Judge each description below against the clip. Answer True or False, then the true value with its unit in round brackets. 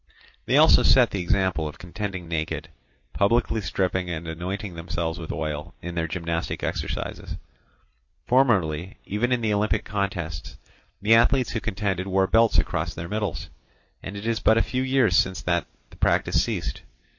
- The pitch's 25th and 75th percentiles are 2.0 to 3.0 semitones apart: False (4.4 semitones)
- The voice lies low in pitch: True (95 Hz)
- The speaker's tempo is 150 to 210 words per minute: True (160 wpm)